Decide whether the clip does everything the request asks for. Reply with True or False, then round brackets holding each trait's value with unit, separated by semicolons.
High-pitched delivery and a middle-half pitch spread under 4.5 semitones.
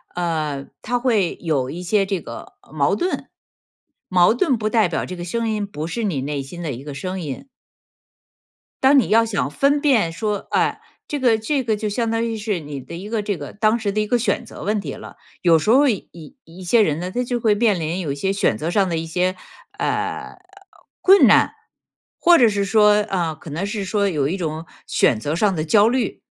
False (195 Hz; 5.3 semitones)